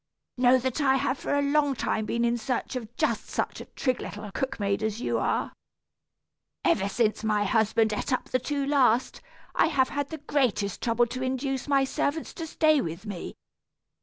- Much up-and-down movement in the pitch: No, average, 4.3 semitones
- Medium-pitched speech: No, very high, 255 Hz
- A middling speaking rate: Yes, average, 195 wpm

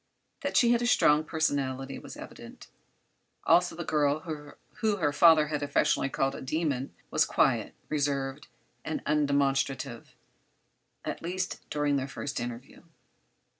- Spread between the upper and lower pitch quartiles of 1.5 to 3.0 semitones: Yes, average, 2.7 semitones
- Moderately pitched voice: Yes, medium, 145 Hz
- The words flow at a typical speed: No, slow, 130 wpm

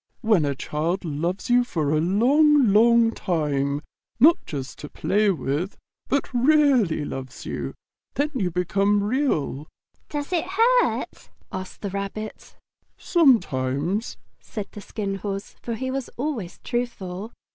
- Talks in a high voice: Yes, high, 205 Hz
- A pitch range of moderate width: No, wide, 7.0 semitones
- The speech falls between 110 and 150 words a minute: Yes, slow, 135 wpm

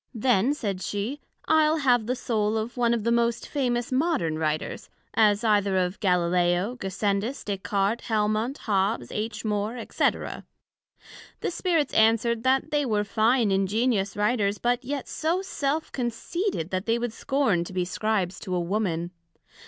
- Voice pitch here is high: Yes, high, 220 Hz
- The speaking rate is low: No, average, 155 wpm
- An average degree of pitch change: Yes, average, 4.0 semitones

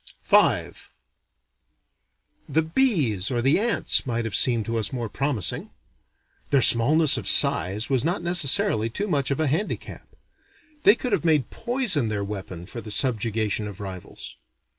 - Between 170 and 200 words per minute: No, average, 150 wpm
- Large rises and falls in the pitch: Yes, wide, 6.8 semitones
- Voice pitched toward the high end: No, low, 125 Hz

